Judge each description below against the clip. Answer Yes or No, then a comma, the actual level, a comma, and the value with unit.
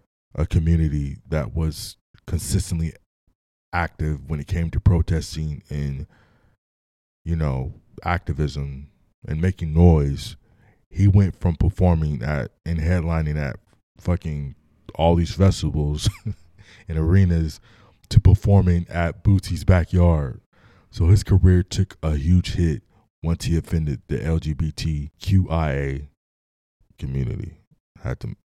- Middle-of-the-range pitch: No, very low, 85 Hz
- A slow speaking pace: Yes, slow, 110 wpm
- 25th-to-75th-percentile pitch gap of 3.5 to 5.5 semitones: Yes, average, 4.0 semitones